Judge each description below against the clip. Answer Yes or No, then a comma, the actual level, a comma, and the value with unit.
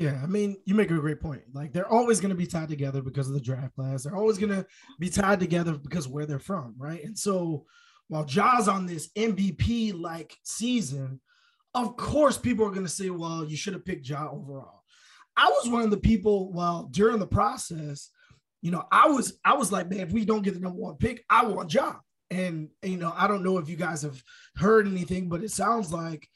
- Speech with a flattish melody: No, average, 5.2 semitones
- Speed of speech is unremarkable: No, fast, 230 wpm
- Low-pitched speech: No, medium, 185 Hz